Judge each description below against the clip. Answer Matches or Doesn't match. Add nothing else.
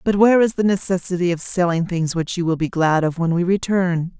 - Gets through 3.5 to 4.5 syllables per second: Doesn't match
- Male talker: Doesn't match